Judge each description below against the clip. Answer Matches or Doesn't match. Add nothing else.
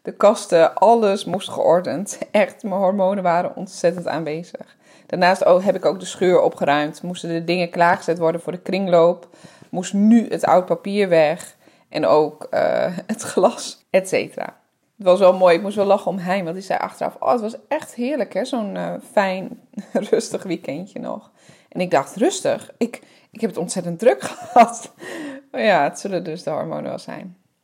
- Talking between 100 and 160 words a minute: Doesn't match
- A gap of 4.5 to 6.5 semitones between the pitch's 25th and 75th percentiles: Matches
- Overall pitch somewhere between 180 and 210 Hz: Matches